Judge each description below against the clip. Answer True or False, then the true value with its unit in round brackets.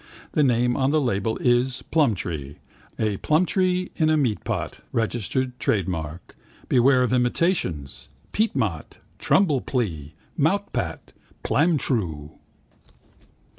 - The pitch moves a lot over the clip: True (7.3 semitones)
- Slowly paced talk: True (95 wpm)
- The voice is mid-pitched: False (125 Hz)